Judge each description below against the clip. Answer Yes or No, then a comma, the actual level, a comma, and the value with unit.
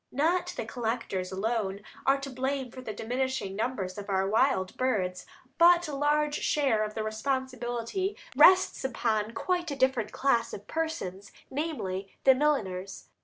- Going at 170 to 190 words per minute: No, average, 150 wpm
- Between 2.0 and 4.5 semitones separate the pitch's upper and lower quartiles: No, average, 5.3 semitones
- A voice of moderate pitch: No, very high, 250 Hz